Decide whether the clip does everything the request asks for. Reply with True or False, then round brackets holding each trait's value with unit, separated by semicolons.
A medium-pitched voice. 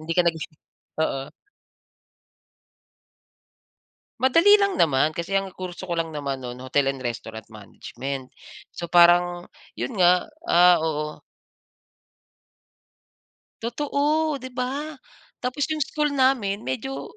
True (175 Hz)